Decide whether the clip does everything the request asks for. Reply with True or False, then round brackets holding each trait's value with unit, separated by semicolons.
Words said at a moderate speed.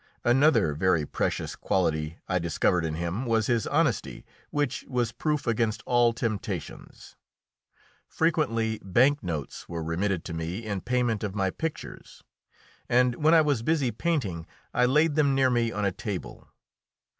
True (150 wpm)